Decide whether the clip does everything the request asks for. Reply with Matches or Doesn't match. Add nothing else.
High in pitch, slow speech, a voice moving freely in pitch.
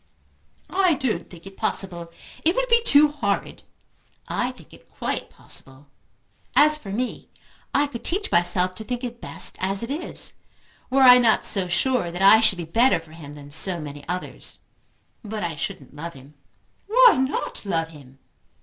Doesn't match